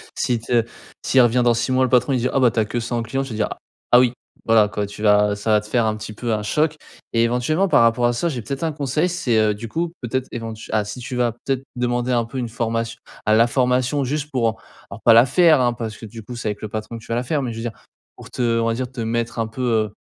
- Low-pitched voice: Yes, low, 120 Hz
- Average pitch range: No, narrow, 2.2 semitones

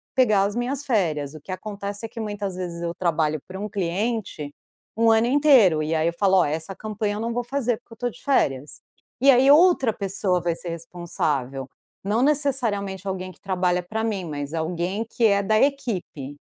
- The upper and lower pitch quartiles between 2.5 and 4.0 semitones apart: No, average, 5.1 semitones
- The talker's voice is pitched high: Yes, high, 195 Hz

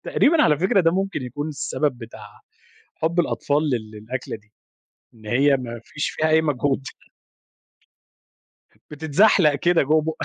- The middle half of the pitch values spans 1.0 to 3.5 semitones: No, average, 4.3 semitones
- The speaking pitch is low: No, medium, 145 Hz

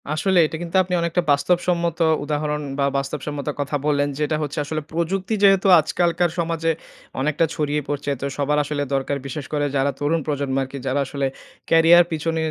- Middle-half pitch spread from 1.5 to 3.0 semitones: Yes, average, 2.7 semitones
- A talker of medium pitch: Yes, medium, 150 Hz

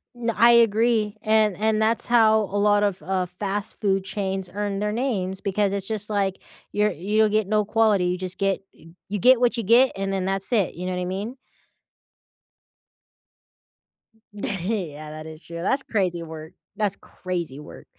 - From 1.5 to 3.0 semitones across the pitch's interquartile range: Yes, average, 2.7 semitones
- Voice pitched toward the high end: Yes, high, 200 Hz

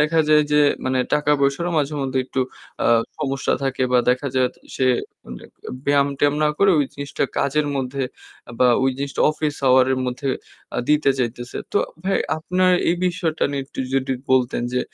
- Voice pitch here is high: No, medium, 140 Hz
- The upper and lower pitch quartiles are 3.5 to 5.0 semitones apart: No, narrow, 2.5 semitones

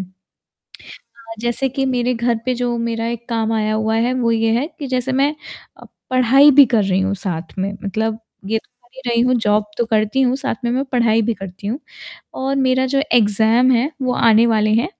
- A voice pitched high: Yes, high, 235 Hz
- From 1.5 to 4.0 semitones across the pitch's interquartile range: Yes, average, 2.9 semitones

